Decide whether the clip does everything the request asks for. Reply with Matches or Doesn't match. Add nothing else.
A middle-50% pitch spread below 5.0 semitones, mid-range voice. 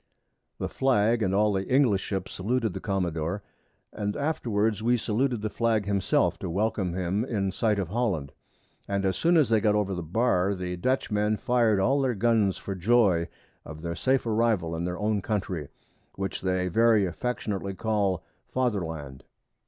Doesn't match